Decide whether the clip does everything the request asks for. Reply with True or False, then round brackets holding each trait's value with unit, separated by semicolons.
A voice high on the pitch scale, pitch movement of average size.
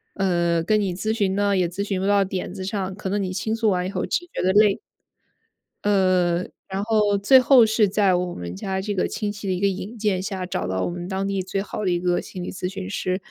False (195 Hz; 2.0 semitones)